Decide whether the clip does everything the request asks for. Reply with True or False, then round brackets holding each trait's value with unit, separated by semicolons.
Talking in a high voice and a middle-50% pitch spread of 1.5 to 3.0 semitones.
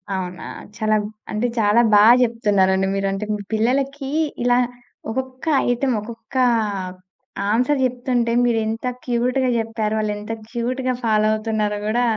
True (230 Hz; 2.7 semitones)